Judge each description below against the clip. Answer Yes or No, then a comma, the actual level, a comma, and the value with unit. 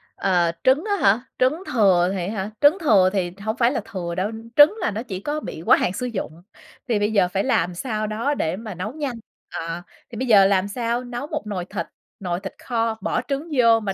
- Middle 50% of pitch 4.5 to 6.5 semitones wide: Yes, average, 5.0 semitones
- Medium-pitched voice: No, high, 215 Hz